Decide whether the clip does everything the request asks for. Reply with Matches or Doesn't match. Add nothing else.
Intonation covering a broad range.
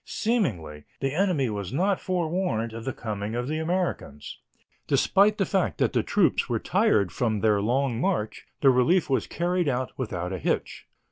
Matches